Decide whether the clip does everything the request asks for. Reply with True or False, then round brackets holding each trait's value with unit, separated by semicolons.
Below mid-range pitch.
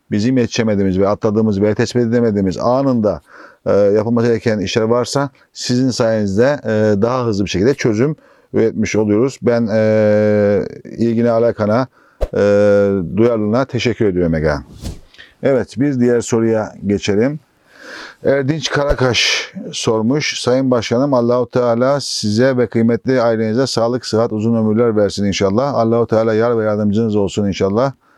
True (115 Hz)